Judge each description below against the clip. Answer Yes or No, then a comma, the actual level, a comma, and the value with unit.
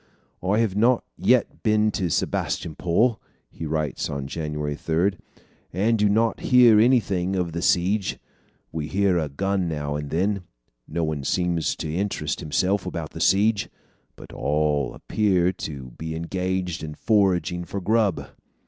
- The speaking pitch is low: Yes, very low, 90 Hz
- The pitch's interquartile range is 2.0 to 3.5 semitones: No, average, 4.5 semitones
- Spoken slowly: No, average, 145 wpm